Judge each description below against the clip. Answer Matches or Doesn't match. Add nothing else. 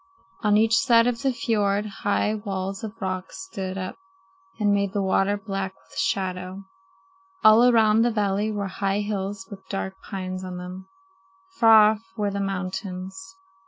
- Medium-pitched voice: Doesn't match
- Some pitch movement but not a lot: Doesn't match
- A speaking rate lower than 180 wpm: Matches